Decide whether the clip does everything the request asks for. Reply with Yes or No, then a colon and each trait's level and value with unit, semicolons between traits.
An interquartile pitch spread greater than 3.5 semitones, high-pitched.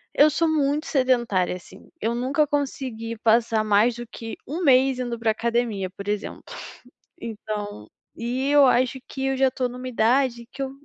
No: average, 3.2 semitones; high, 240 Hz